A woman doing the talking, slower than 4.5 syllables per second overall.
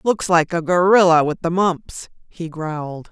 Yes: female; 4.3 syllables/s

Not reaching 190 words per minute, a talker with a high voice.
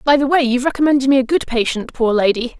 No: fast, 255 wpm; very high, 260 Hz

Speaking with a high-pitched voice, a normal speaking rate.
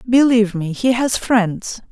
Yes: high, 225 Hz; average, 155 wpm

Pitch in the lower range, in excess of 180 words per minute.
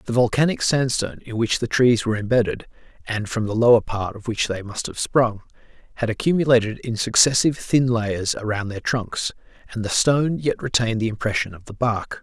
Yes: low, 115 Hz; average, 190 wpm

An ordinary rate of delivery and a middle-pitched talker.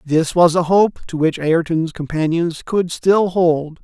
Yes: average, 170 wpm; medium, 170 Hz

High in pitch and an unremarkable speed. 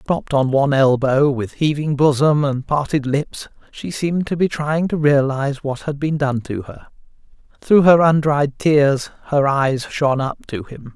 No: medium, 140 Hz; average, 180 wpm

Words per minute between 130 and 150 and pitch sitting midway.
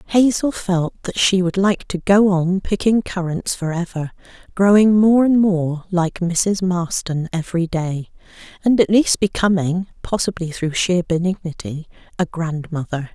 Yes: average, 145 wpm; medium, 180 Hz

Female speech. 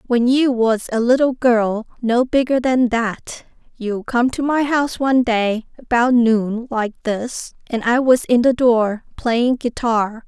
Yes: female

